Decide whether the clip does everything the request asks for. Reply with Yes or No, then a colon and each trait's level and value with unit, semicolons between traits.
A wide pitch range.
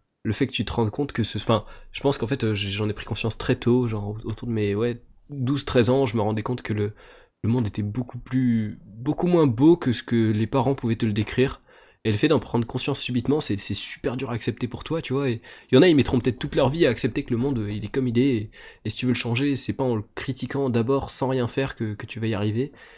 No: average, 3.5 semitones